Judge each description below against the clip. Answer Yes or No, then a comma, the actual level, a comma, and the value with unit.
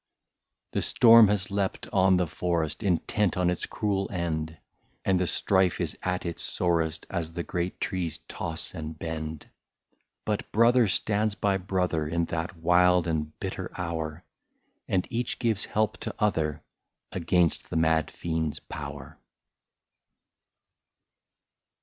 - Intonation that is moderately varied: Yes, average, 3.3 semitones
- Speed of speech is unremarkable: No, slow, 130 wpm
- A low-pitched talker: Yes, very low, 90 Hz